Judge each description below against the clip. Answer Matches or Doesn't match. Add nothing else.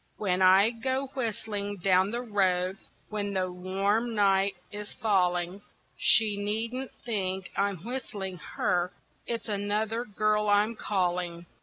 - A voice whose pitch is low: Doesn't match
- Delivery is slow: Matches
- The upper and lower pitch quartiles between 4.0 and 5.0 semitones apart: Doesn't match